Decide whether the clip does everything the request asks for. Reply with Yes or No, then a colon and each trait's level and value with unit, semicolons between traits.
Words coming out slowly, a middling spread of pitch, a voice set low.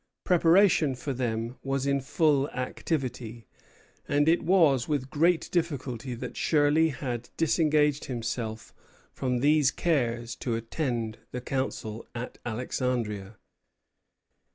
Yes: slow, 110 wpm; average, 4.1 semitones; low, 130 Hz